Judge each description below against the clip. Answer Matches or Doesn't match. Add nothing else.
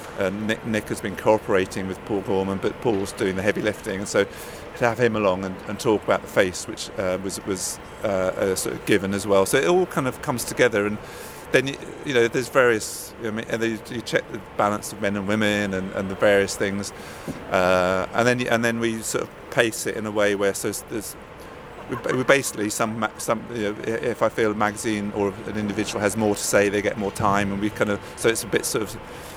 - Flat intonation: Matches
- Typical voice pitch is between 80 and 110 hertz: Matches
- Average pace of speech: Doesn't match